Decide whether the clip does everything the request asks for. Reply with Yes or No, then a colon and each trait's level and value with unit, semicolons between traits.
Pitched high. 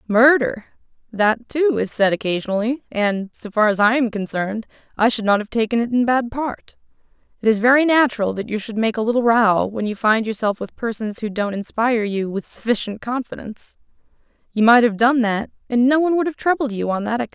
Yes: high, 230 Hz